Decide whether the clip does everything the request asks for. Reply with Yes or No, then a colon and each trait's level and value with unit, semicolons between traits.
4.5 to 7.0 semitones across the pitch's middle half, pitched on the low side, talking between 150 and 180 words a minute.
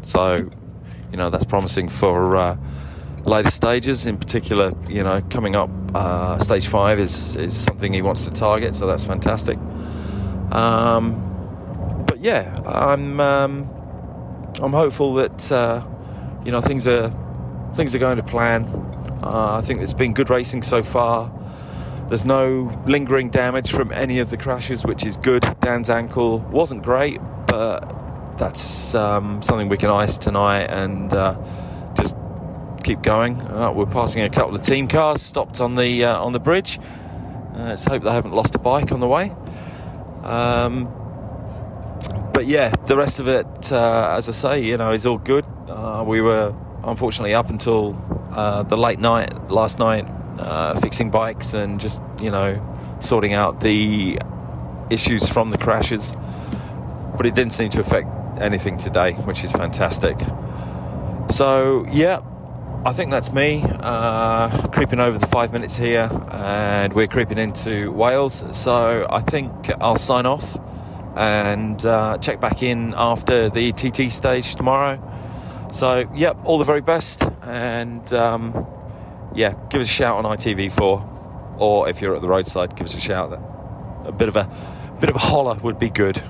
No: average, 3.5 semitones; low, 110 Hz; average, 165 wpm